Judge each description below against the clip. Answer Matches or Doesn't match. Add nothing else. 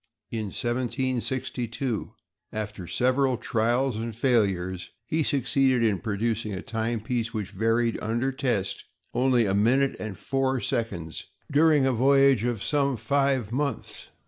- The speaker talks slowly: Matches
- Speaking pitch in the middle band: Doesn't match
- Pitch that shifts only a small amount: Doesn't match